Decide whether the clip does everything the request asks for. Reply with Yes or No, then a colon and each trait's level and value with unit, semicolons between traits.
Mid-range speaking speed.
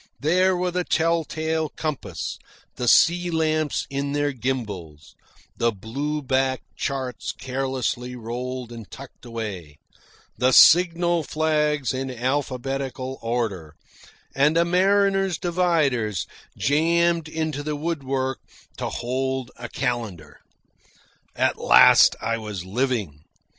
No: slow, 110 wpm